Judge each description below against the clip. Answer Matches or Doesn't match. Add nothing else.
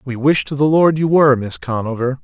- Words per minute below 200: Doesn't match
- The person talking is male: Matches